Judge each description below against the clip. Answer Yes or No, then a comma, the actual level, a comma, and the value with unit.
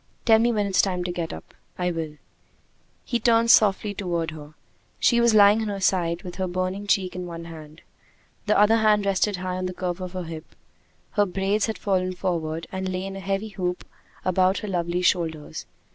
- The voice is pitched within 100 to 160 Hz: No, medium, 185 Hz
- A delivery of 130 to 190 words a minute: No, fast, 205 wpm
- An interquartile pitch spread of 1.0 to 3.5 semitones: Yes, narrow, 2.6 semitones